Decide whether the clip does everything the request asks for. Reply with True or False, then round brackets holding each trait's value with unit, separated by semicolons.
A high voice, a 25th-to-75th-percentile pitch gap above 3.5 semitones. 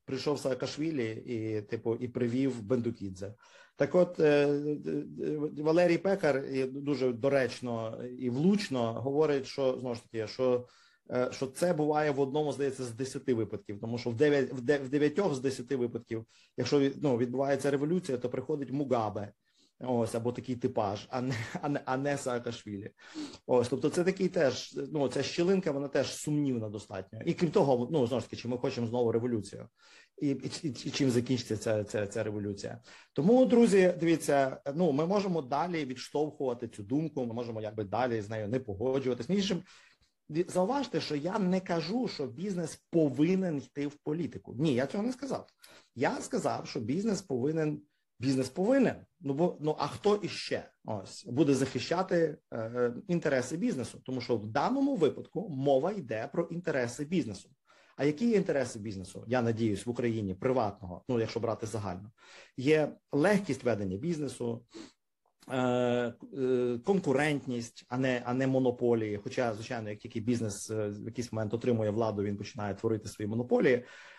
False (130 Hz; 4.3 semitones)